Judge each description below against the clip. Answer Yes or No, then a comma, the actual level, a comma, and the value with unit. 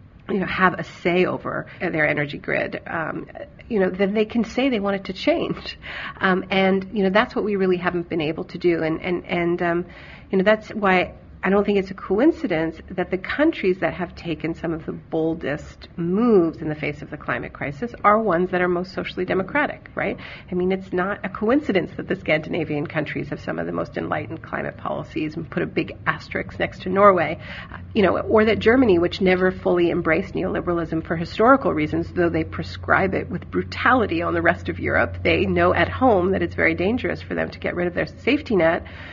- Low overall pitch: No, medium, 180 Hz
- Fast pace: Yes, fast, 215 wpm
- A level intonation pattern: No, average, 3.6 semitones